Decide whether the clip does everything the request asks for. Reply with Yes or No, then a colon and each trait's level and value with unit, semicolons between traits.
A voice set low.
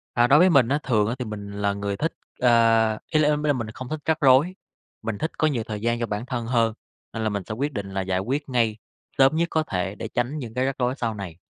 Yes: low, 120 Hz